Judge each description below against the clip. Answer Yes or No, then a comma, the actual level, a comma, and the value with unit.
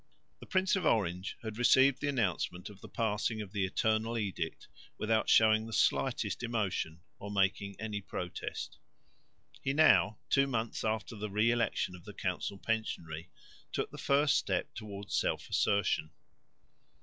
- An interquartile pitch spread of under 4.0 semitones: Yes, average, 3.0 semitones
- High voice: No, low, 110 Hz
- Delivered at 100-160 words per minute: Yes, average, 150 wpm